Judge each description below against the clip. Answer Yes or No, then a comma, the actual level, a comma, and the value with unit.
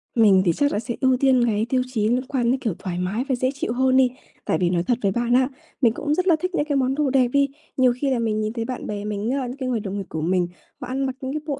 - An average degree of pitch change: Yes, average, 3.8 semitones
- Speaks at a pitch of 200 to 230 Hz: No, very high, 250 Hz